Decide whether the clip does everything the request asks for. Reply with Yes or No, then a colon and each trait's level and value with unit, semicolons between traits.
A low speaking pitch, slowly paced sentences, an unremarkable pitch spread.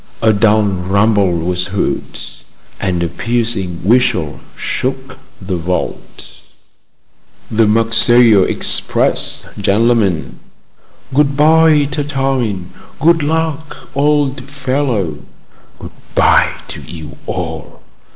No: low, 115 Hz; slow, 95 wpm; wide, 6.4 semitones